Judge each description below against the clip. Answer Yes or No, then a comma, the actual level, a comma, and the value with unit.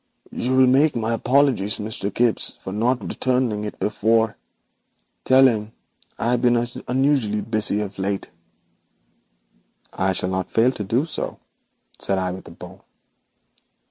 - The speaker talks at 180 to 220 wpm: No, average, 145 wpm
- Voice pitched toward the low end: Yes, low, 110 Hz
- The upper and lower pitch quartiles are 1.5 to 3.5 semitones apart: No, average, 3.9 semitones